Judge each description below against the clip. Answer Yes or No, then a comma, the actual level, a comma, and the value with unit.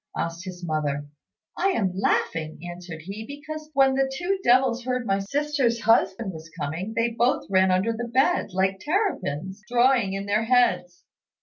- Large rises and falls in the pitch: Yes, wide, 6.0 semitones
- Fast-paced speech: No, average, 165 wpm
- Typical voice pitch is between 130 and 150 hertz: No, high, 220 Hz